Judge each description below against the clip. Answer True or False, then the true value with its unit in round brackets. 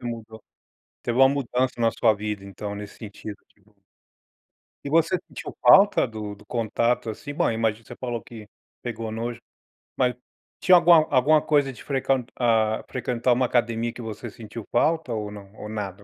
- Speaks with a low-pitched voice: True (115 Hz)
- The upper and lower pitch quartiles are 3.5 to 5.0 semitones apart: False (3.1 semitones)